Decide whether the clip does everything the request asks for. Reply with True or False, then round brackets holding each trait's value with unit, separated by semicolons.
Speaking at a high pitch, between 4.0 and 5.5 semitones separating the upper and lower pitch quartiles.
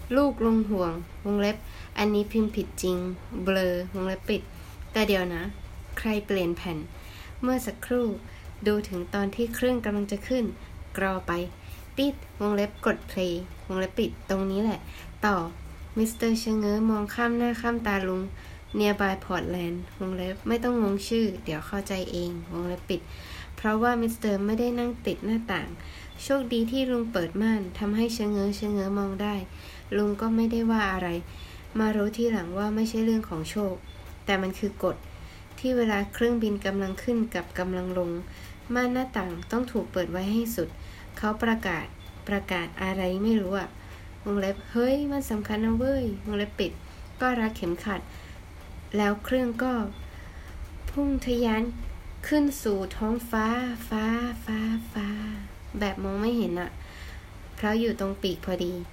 False (205 Hz; 3.6 semitones)